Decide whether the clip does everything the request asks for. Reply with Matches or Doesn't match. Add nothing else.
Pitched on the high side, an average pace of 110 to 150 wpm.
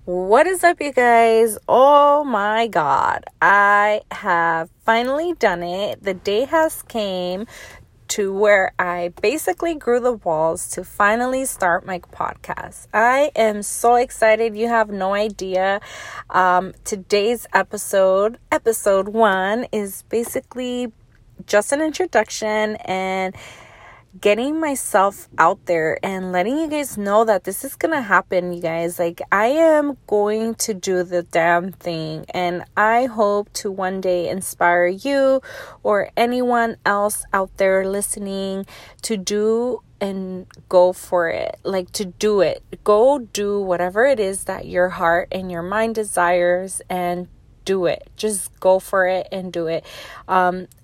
Matches